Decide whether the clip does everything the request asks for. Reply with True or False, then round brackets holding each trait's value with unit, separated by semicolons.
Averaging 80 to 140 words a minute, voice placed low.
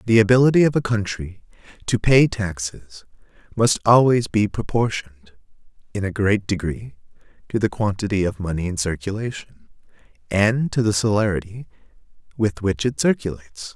True (135 wpm; 105 Hz)